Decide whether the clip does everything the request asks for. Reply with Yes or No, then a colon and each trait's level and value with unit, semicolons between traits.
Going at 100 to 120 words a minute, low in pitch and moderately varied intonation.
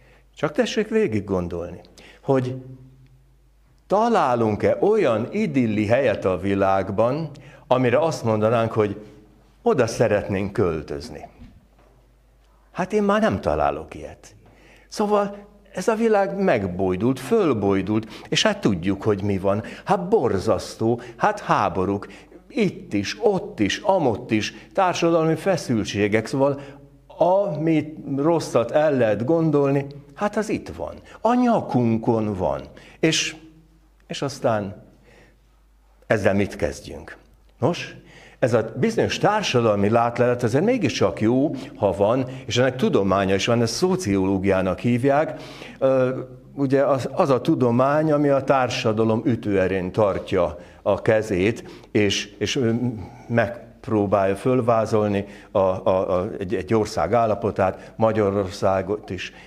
No: average, 110 wpm; low, 120 Hz; wide, 6.9 semitones